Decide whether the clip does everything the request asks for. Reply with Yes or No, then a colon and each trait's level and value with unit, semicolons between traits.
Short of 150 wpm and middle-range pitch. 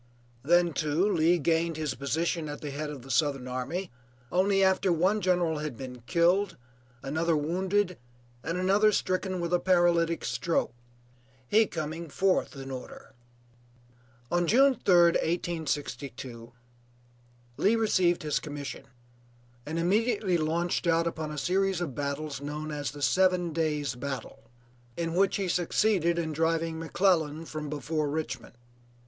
Yes: average, 140 wpm; medium, 165 Hz